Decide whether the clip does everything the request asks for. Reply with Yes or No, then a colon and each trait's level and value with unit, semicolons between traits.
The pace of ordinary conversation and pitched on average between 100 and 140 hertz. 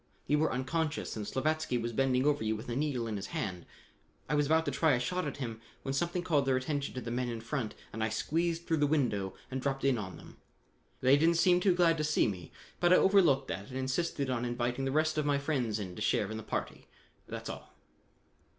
No: fast, 240 wpm; low, 135 Hz